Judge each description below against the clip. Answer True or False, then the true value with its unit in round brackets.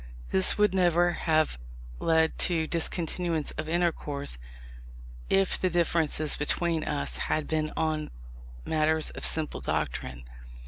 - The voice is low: False (160 Hz)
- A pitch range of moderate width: False (2.0 semitones)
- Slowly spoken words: True (120 wpm)